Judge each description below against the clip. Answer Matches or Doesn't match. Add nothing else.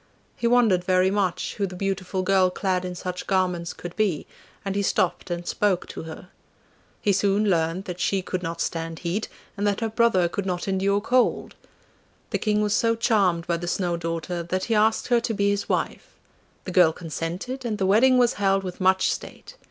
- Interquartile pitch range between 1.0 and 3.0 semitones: Matches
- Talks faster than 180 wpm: Matches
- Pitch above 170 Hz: Matches